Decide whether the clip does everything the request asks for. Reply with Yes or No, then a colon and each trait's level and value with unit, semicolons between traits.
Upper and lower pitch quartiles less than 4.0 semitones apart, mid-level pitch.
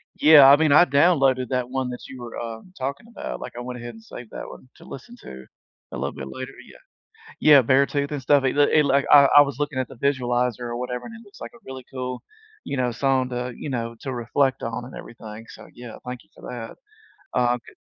No: narrow, 2.5 semitones; low, 130 Hz